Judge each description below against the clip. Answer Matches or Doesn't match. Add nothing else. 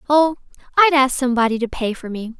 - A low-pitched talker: Doesn't match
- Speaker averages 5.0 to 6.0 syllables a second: Doesn't match